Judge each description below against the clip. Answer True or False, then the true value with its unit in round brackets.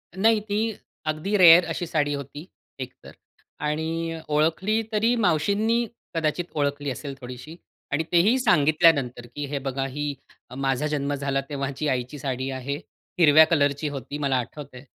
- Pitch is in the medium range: True (150 Hz)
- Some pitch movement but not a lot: True (3.3 semitones)